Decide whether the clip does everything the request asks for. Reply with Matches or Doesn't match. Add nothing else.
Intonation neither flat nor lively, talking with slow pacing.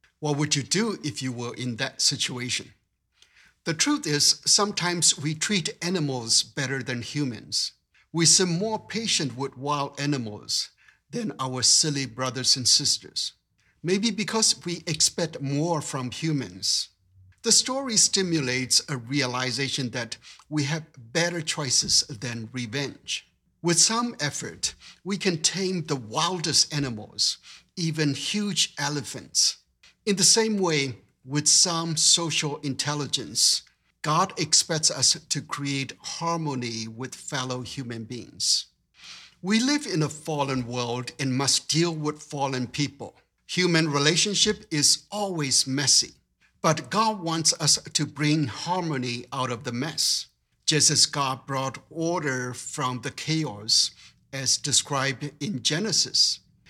Matches